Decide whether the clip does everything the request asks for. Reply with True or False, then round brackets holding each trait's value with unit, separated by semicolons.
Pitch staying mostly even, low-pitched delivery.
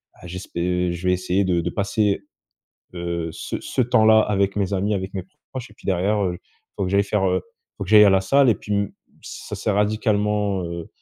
True (2.3 semitones; 100 Hz)